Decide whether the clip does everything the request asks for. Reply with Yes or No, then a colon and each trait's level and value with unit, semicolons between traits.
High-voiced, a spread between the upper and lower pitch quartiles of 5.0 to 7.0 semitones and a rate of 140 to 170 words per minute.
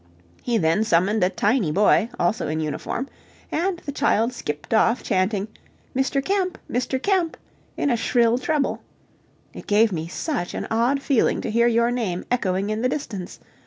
Yes: high, 230 Hz; wide, 5.4 semitones; average, 165 wpm